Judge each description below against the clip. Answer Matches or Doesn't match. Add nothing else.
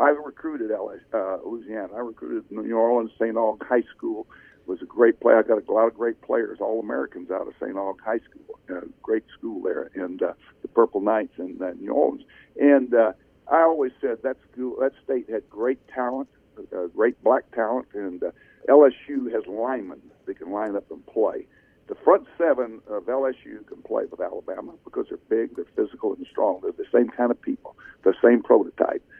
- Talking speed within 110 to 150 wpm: Doesn't match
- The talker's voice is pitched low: Doesn't match